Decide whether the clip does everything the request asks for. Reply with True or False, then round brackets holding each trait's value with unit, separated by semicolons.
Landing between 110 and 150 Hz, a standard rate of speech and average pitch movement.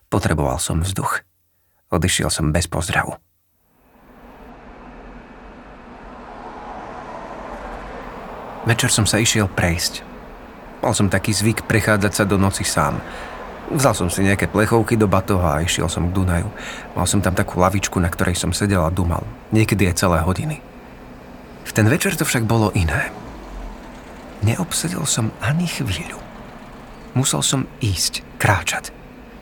False (100 Hz; 130 wpm; 4.8 semitones)